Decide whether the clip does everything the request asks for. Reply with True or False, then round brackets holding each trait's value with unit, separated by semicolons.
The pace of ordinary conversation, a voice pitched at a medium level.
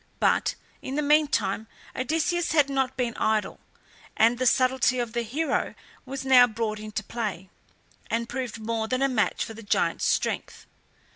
False (160 wpm; 245 Hz)